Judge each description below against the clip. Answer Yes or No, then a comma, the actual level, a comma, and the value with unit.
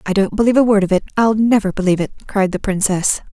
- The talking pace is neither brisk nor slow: No, fast, 235 wpm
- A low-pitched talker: No, high, 205 Hz